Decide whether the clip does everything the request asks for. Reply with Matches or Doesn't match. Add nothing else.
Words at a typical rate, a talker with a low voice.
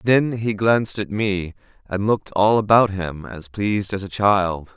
Matches